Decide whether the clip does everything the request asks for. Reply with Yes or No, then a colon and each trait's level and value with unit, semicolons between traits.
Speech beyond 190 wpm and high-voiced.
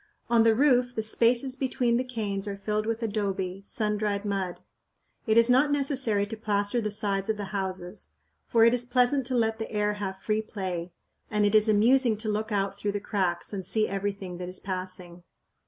Yes: fast, 205 wpm; high, 210 Hz